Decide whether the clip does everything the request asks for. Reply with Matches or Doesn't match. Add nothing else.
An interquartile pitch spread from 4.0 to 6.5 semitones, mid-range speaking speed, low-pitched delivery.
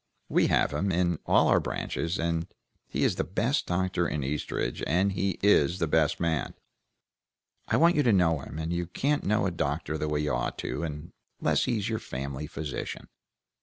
Matches